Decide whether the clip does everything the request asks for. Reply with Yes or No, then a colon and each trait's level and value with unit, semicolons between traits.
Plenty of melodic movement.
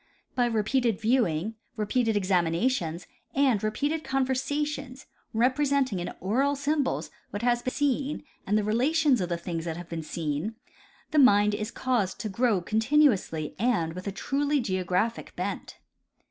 Yes: wide, 6.1 semitones